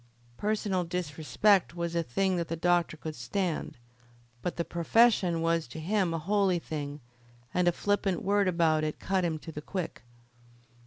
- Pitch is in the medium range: Yes, medium, 170 Hz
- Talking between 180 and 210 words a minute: No, average, 165 wpm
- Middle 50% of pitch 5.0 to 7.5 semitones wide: No, average, 3.1 semitones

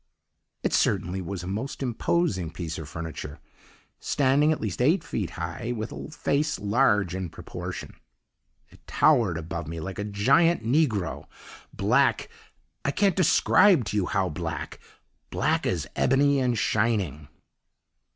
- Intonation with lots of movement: Yes, wide, 7.9 semitones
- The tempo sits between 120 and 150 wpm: Yes, average, 140 wpm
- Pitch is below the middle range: Yes, low, 105 Hz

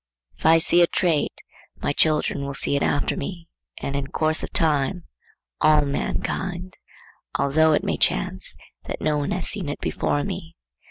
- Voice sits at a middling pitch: Yes, medium, 155 Hz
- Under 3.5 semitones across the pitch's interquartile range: Yes, average, 3.0 semitones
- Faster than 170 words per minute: No, average, 165 wpm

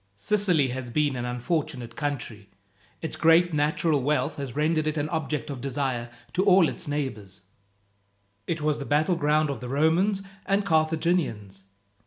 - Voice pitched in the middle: Yes, medium, 150 Hz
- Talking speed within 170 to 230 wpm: No, average, 150 wpm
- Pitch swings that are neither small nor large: Yes, average, 3.9 semitones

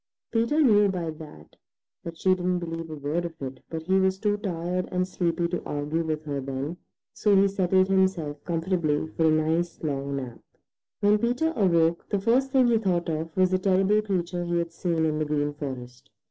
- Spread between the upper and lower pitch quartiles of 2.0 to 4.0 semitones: Yes, average, 3.5 semitones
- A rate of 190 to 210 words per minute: Yes, average, 200 wpm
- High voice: No, medium, 170 Hz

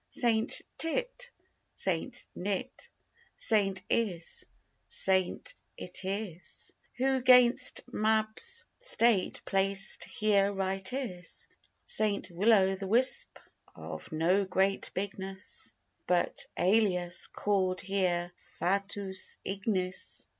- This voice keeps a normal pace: No, slow, 90 wpm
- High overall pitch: Yes, high, 195 Hz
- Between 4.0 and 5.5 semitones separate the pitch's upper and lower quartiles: No, average, 2.9 semitones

